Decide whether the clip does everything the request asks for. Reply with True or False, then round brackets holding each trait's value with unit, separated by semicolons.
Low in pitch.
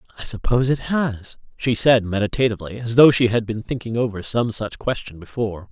True (115 Hz)